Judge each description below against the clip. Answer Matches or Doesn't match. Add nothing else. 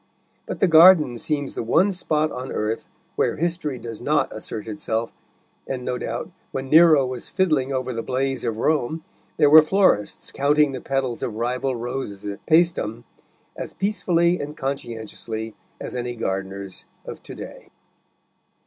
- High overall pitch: Doesn't match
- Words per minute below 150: Doesn't match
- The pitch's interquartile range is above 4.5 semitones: Matches